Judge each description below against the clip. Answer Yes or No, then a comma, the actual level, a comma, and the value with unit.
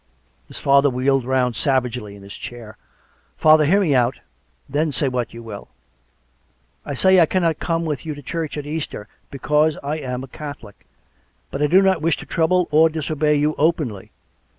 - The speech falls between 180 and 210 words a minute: Yes, average, 190 wpm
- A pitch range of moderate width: Yes, average, 3.9 semitones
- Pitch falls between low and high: Yes, medium, 145 Hz